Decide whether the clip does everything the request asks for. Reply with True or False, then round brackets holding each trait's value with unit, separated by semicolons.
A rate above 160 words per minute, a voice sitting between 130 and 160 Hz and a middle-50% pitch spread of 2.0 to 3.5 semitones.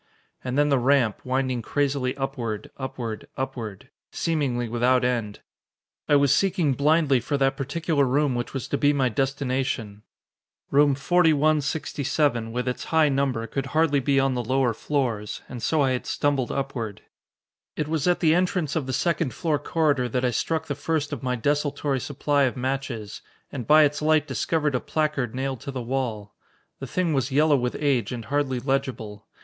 True (175 wpm; 135 Hz; 2.9 semitones)